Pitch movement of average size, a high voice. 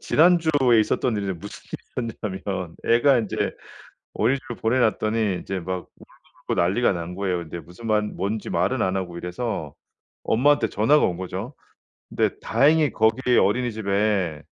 No: average, 4.8 semitones; low, 110 Hz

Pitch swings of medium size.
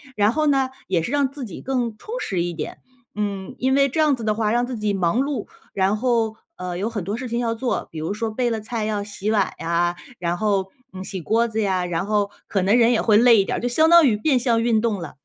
Yes: average, 3.7 semitones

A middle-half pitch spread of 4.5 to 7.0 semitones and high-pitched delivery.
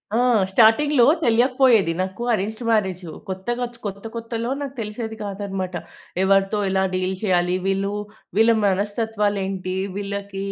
No: average, 2.9 semitones; high, 200 Hz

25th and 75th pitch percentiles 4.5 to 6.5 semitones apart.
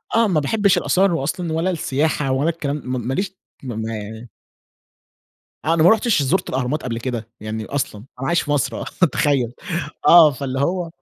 Yes: average, 5.1 semitones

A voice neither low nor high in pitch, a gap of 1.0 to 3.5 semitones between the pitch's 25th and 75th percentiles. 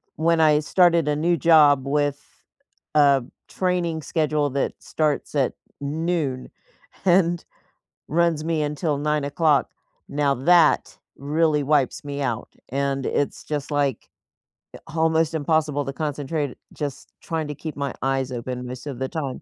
Yes: medium, 150 Hz; narrow, 2.5 semitones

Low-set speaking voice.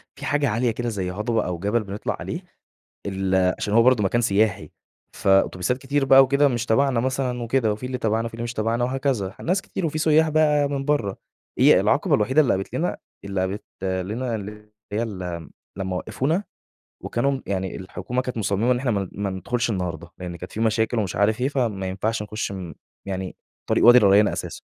Yes: low, 110 Hz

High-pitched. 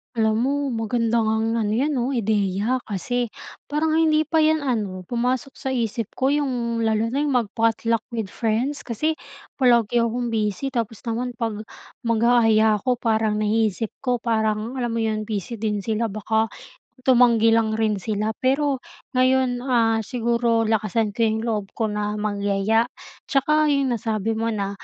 Yes: high, 230 Hz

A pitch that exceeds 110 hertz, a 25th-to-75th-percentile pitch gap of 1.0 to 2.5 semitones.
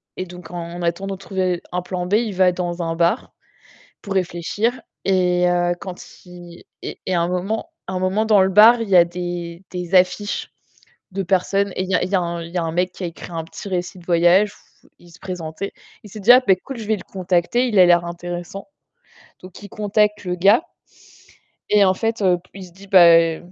Yes: medium, 185 Hz; narrow, 2.2 semitones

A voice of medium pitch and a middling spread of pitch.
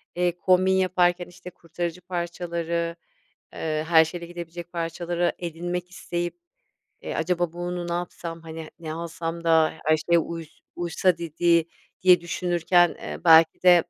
No: medium, 170 Hz; narrow, 1.1 semitones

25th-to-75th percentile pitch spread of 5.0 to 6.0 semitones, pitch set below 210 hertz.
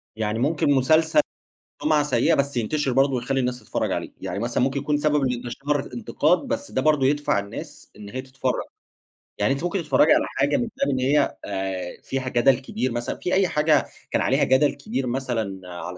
No: average, 3.6 semitones; low, 135 Hz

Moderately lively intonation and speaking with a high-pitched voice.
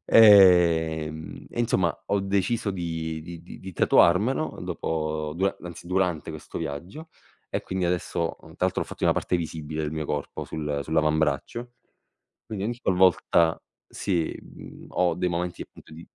No: average, 3.1 semitones; very low, 85 Hz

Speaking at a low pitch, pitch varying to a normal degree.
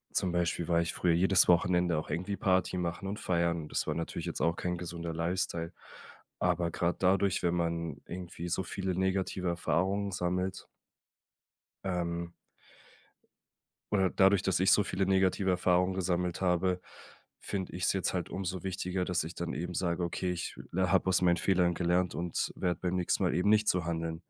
No: very low, 90 Hz; narrow, 1.6 semitones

